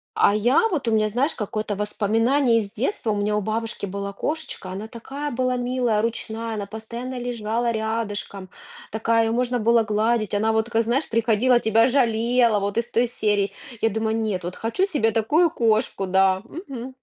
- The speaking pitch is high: Yes, high, 225 Hz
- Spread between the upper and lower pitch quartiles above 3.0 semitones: No, narrow, 2.5 semitones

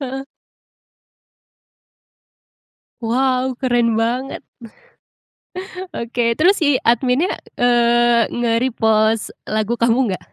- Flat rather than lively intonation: Yes, narrow, 2.0 semitones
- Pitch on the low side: No, high, 240 Hz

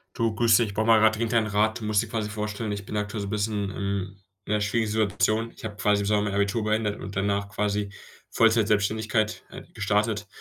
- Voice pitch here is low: Yes, low, 105 Hz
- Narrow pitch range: Yes, narrow, 1.3 semitones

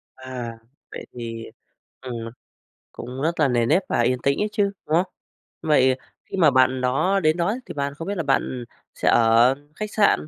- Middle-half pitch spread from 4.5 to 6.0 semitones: Yes, average, 5.1 semitones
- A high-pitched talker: No, low, 135 Hz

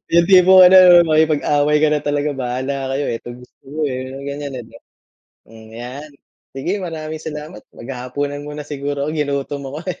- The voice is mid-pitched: Yes, medium, 145 Hz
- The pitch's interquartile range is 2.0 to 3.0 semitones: Yes, narrow, 2.4 semitones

